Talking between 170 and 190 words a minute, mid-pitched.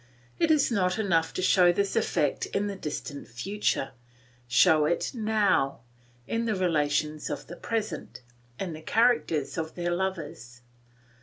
No: average, 145 wpm; medium, 175 Hz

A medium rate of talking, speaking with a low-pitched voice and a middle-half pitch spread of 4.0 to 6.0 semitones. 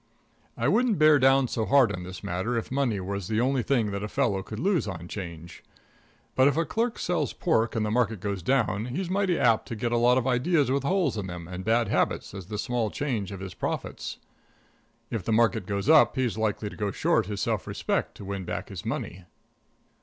No: fast, 225 wpm; low, 115 Hz; average, 5.2 semitones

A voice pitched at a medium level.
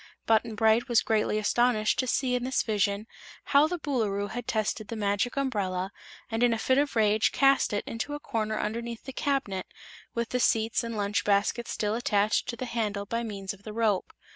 No: high, 225 Hz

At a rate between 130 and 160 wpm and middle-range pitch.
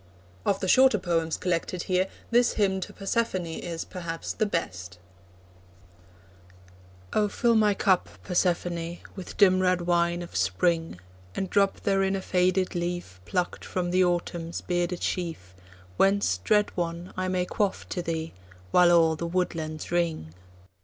Yes: average, 145 wpm; medium, 175 Hz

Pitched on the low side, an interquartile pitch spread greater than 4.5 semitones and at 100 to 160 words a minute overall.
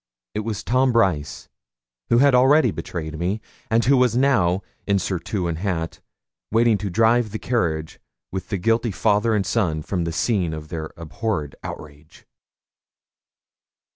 Yes: low, 100 Hz; wide, 5.6 semitones; average, 150 wpm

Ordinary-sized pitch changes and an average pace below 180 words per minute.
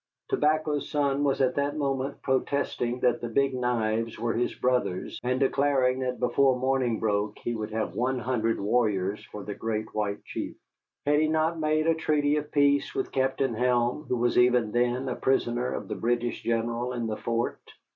No: average, 3.0 semitones; average, 185 wpm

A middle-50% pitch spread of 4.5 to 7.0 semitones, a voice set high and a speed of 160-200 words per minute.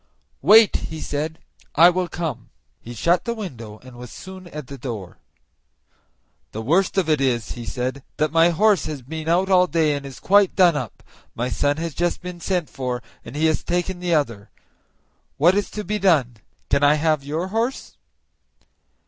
No: average, 5.2 semitones; medium, 160 Hz; average, 185 wpm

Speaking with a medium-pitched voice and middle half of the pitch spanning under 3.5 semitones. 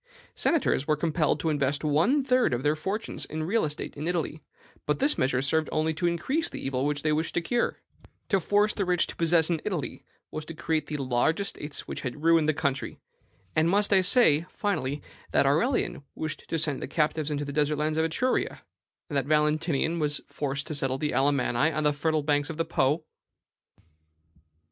Yes: medium, 155 Hz; average, 2.7 semitones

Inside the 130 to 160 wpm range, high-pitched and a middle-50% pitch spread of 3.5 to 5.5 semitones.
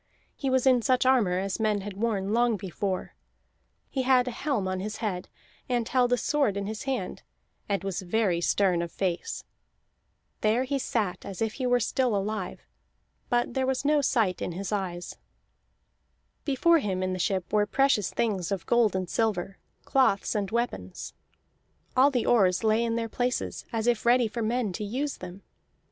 No: average, 180 wpm; high, 220 Hz; average, 4.3 semitones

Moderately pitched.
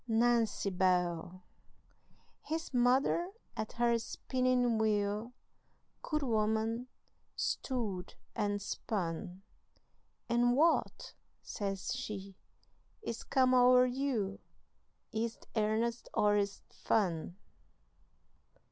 No: high, 225 Hz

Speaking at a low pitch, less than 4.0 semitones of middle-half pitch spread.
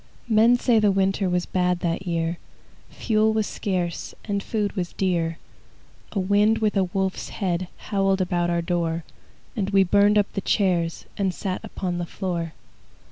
No: high, 190 Hz; narrow, 2.6 semitones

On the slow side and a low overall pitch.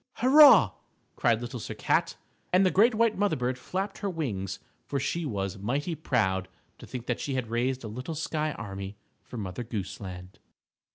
No: average, 185 wpm; low, 130 Hz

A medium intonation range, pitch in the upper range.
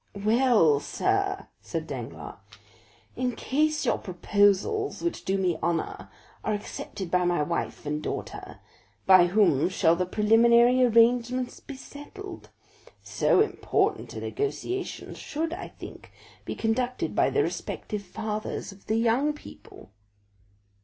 No: wide, 6.3 semitones; high, 225 Hz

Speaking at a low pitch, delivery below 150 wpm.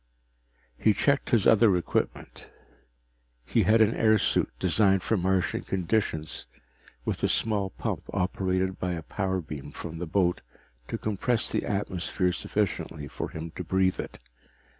Yes: very low, 95 Hz; average, 140 wpm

